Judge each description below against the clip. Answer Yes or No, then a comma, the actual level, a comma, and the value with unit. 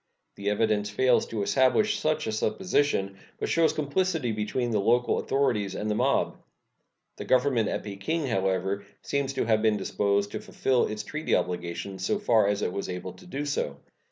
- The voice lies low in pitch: Yes, low, 110 Hz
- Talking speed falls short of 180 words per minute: No, average, 185 wpm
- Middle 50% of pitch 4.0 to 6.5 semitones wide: Yes, average, 5.2 semitones